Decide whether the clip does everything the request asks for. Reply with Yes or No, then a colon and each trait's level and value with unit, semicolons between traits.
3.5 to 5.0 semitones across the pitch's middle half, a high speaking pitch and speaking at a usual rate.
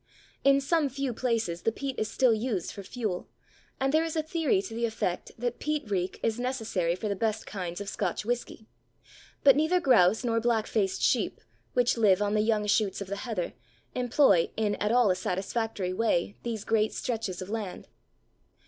Yes: average, 3.8 semitones; high, 225 Hz; average, 190 wpm